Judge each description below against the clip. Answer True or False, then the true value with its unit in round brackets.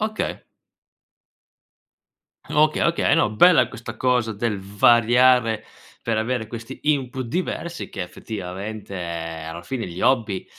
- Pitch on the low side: True (115 Hz)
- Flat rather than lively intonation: False (4.4 semitones)